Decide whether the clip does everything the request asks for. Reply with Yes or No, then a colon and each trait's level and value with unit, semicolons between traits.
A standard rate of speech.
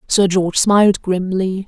Yes: average, 145 wpm